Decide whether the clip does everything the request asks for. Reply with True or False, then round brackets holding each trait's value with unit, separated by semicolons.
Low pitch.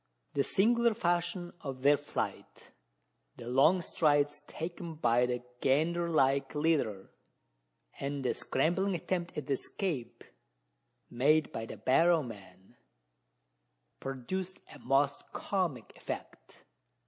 False (145 Hz)